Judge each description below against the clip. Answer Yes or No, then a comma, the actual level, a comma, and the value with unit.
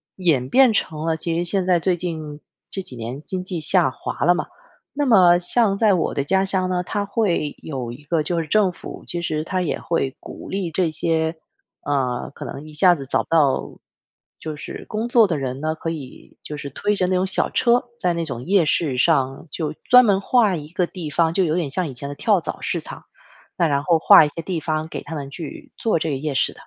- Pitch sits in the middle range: Yes, medium, 165 Hz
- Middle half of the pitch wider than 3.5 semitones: Yes, average, 3.9 semitones